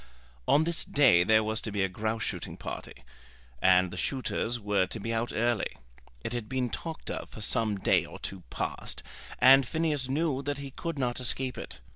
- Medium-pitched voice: No, low, 120 Hz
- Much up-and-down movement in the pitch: No, average, 4.3 semitones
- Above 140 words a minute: Yes, average, 195 wpm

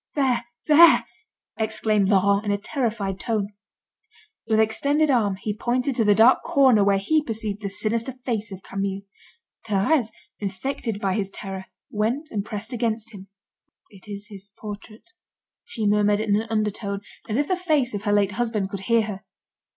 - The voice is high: Yes, high, 215 Hz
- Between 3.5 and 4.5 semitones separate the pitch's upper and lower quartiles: No, average, 2.9 semitones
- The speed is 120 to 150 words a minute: No, average, 165 wpm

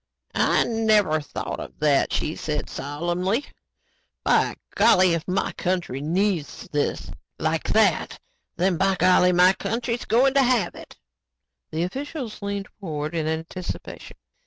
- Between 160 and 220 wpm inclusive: No, slow, 135 wpm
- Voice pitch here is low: No, medium, 180 Hz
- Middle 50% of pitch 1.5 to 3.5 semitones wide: No, average, 4.9 semitones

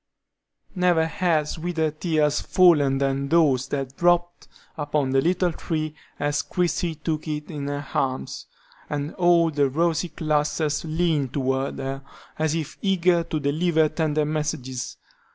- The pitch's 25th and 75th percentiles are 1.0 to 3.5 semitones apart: Yes, average, 2.9 semitones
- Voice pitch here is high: No, medium, 155 Hz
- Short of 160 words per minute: Yes, slow, 135 wpm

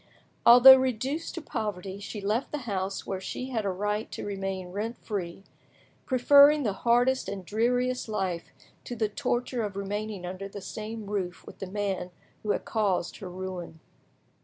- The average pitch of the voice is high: Yes, high, 210 Hz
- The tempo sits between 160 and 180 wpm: Yes, average, 165 wpm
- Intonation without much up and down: No, average, 3.9 semitones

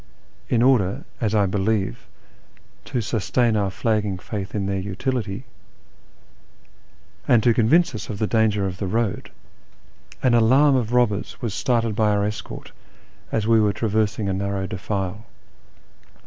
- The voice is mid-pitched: No, low, 105 Hz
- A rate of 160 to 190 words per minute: No, average, 145 wpm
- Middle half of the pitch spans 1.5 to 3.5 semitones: Yes, average, 2.8 semitones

